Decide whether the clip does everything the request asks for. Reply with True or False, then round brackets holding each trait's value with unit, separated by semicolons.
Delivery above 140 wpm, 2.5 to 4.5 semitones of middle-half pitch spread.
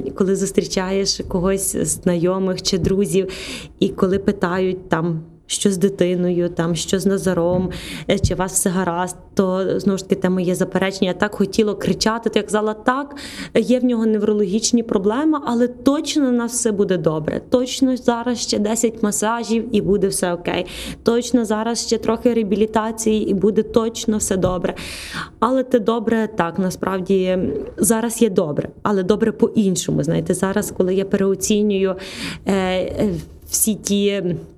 True (150 wpm; 3.2 semitones)